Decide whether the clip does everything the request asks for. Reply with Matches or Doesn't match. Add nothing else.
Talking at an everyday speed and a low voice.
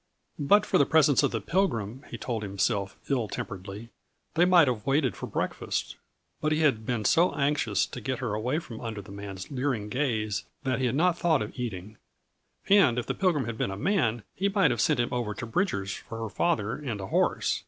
Doesn't match